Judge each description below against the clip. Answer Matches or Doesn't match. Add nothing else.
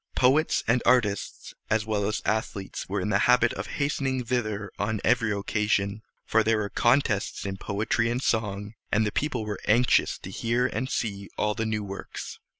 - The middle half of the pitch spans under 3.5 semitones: Matches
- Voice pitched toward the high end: Doesn't match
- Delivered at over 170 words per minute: Matches